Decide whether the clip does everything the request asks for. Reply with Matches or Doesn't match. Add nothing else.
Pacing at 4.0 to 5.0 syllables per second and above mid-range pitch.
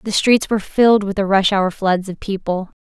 Doesn't match